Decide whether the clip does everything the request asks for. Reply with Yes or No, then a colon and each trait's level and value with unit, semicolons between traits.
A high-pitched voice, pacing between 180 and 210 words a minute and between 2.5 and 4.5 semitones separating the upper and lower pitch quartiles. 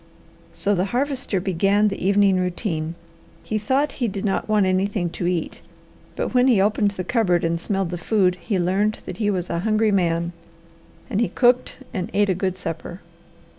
Yes: high, 195 Hz; average, 185 wpm; average, 3.1 semitones